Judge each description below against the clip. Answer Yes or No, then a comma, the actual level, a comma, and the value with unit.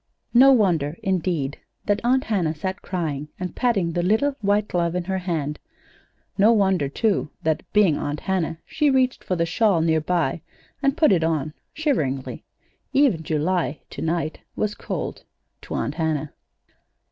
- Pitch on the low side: No, medium, 180 Hz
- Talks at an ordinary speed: Yes, average, 160 wpm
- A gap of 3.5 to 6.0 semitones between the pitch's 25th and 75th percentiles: Yes, average, 5.0 semitones